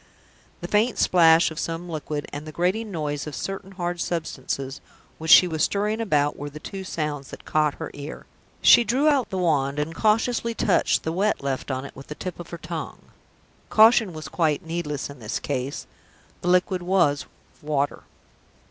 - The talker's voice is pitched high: No, medium, 165 Hz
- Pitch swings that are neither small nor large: Yes, average, 4.5 semitones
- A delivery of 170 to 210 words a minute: Yes, average, 185 wpm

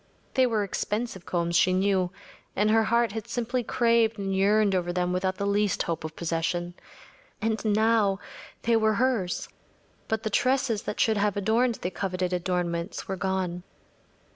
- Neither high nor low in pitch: No, high, 200 Hz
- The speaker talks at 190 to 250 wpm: No, average, 165 wpm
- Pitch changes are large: No, average, 3.5 semitones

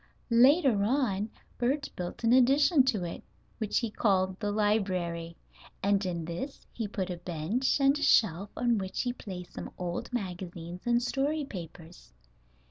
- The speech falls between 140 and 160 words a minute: Yes, average, 155 wpm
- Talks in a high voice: Yes, high, 205 Hz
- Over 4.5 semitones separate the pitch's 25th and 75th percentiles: Yes, wide, 5.6 semitones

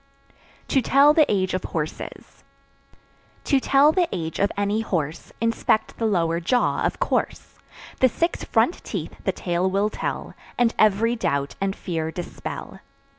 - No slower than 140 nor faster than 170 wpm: Yes, average, 150 wpm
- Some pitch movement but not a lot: No, wide, 5.8 semitones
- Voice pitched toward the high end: Yes, high, 200 Hz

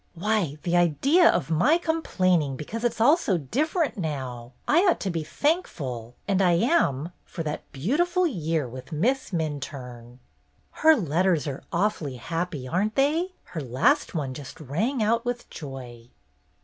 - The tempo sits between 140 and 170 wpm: Yes, average, 160 wpm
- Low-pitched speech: No, medium, 170 Hz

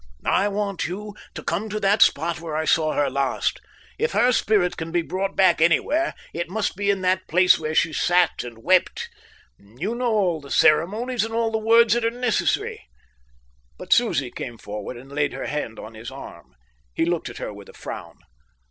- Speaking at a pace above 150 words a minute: Yes, average, 200 wpm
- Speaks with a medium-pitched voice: Yes, medium, 180 Hz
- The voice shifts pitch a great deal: Yes, wide, 6.2 semitones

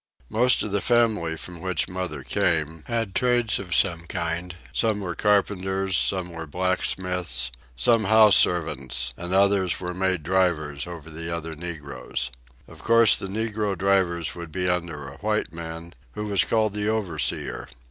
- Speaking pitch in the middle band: No, very low, 90 Hz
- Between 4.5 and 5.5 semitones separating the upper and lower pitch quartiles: No, average, 3.6 semitones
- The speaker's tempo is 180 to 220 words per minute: No, average, 155 wpm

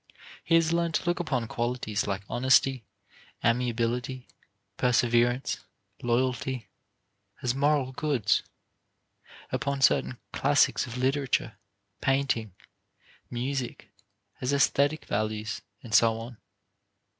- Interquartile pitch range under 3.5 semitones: Yes, average, 2.9 semitones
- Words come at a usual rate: No, slow, 100 wpm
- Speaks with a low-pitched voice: Yes, low, 125 Hz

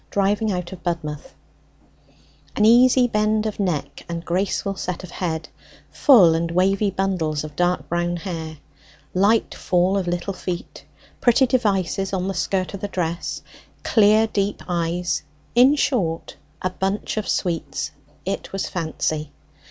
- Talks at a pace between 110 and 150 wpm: Yes, average, 145 wpm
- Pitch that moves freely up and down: No, average, 3.2 semitones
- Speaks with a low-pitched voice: No, medium, 185 Hz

